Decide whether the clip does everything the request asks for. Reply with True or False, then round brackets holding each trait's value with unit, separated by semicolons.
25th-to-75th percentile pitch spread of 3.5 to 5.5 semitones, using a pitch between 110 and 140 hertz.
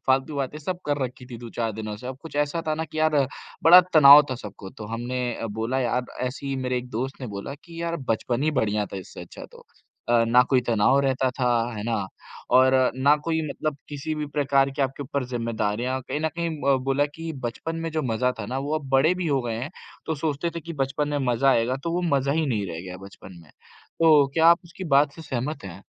True (4.2 semitones; 135 Hz)